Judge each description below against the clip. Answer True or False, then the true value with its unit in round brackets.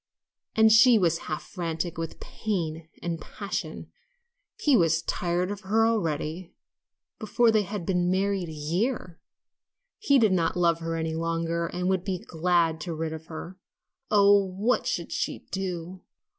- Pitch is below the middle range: False (180 Hz)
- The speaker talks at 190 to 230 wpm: False (160 wpm)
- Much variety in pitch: False (3.5 semitones)